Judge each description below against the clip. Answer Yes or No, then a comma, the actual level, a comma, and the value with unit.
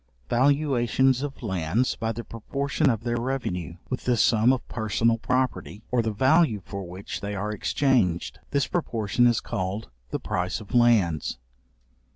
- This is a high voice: No, low, 115 Hz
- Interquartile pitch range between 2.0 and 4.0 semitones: No, average, 4.4 semitones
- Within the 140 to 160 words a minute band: Yes, average, 155 wpm